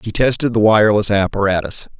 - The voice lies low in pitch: Yes, low, 105 Hz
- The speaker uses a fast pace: No, average, 150 wpm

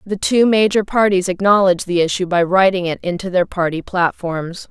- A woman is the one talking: Yes, female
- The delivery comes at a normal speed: Yes, average, 180 wpm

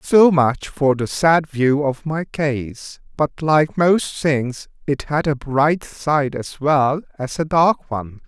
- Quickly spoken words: No, average, 175 wpm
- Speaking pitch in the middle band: Yes, medium, 145 Hz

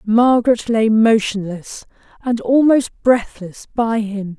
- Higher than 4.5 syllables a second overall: No, 3.6 syllables/s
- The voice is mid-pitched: No, high, 225 Hz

